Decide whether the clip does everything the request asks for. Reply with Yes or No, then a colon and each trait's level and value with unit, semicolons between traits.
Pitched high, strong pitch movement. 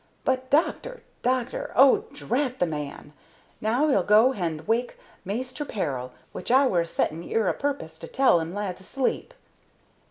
Yes: high, 225 Hz; wide, 7.5 semitones